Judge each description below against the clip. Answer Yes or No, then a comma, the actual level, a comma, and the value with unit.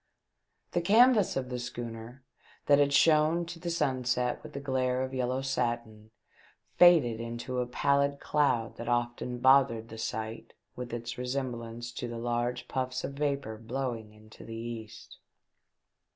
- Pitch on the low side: Yes, low, 125 Hz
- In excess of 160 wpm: No, average, 150 wpm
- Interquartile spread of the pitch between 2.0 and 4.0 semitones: Yes, average, 3.0 semitones